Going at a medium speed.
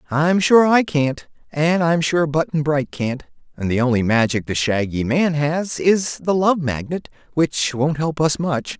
Yes: average, 185 wpm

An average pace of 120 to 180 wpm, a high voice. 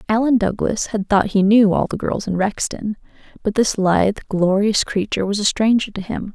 No: average, 200 wpm; high, 205 Hz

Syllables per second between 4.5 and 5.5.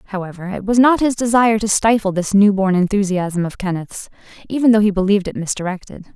No: 6.3 syllables/s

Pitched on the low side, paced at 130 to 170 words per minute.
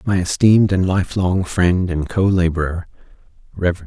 Yes: very low, 90 Hz; average, 140 wpm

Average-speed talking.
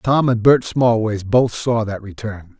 Yes: average, 185 wpm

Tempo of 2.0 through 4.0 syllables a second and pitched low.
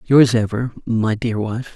Yes: 3.9 syllables/s; low, 115 Hz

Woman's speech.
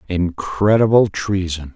No: male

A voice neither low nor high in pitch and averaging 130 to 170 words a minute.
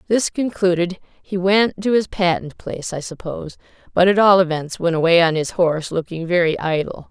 No: medium, 180 Hz; average, 185 wpm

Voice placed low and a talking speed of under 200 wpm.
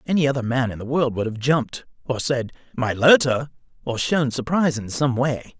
No: low, 130 Hz; fast, 205 wpm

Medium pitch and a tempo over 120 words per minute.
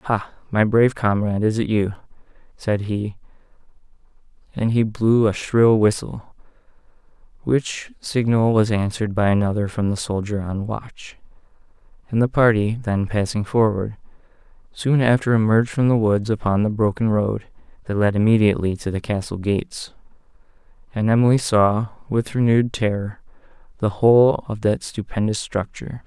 No: low, 110 Hz; average, 140 wpm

